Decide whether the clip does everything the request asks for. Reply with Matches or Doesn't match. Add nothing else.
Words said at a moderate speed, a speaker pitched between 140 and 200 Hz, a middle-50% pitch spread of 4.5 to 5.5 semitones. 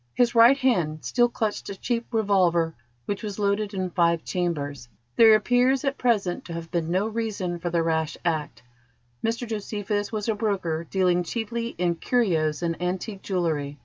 Matches